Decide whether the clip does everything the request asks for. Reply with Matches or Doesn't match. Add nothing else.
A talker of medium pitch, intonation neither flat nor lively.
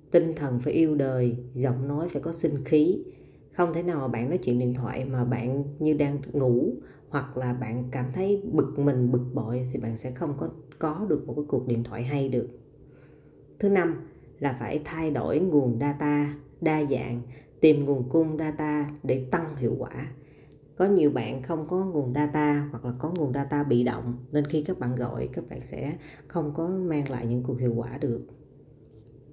Matches